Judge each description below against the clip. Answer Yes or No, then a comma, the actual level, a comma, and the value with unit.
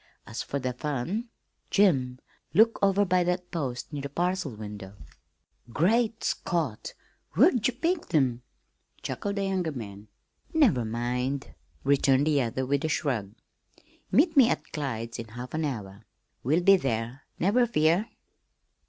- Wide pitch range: Yes, wide, 7.8 semitones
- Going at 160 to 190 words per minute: No, average, 145 wpm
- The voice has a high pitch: No, medium, 145 Hz